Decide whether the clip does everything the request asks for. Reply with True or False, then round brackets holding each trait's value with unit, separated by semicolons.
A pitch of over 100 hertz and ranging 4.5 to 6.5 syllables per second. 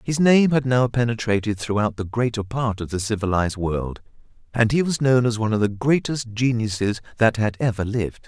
True (115 Hz; 5.5 syllables/s)